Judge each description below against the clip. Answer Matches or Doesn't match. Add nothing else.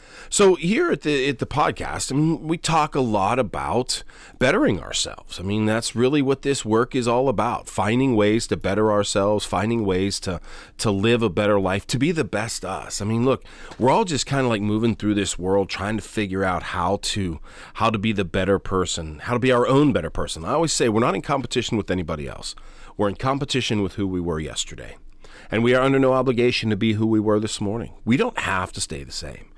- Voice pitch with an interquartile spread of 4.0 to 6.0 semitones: Matches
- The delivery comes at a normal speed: Doesn't match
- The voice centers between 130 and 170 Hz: Doesn't match